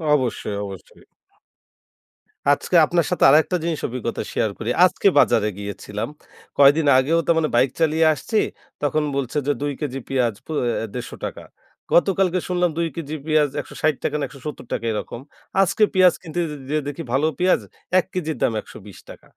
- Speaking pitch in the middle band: Yes, medium, 150 Hz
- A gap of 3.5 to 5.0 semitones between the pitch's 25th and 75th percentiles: Yes, average, 4.6 semitones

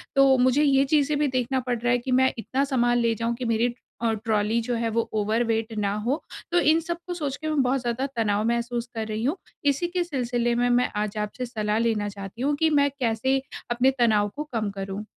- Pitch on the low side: No, high, 240 Hz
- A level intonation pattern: No, average, 3.3 semitones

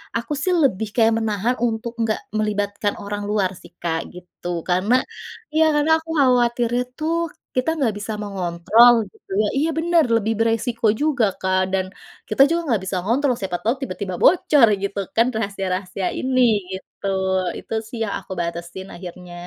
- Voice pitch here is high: Yes, high, 220 Hz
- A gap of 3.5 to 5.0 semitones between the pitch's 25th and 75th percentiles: Yes, average, 4.7 semitones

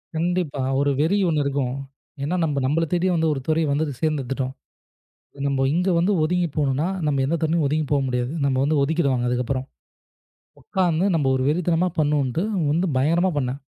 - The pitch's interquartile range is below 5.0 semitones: Yes, average, 3.4 semitones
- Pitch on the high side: No, medium, 150 Hz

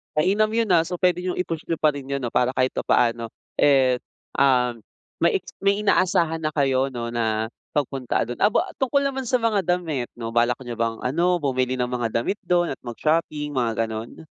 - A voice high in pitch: No, medium, 140 Hz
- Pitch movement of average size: No, wide, 6.4 semitones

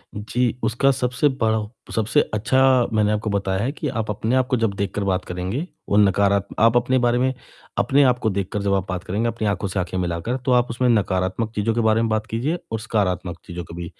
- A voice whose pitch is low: Yes, low, 110 Hz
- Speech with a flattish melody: No, average, 3.7 semitones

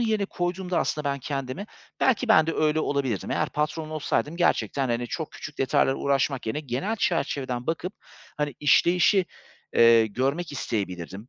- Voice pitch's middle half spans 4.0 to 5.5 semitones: Yes, average, 5.0 semitones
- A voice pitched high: No, medium, 150 Hz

